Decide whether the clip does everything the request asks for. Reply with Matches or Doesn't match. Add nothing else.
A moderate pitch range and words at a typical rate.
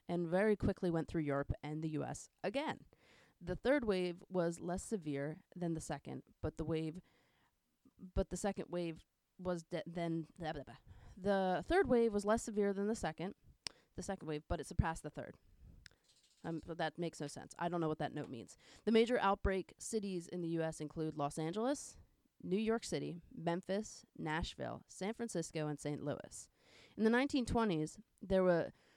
Matches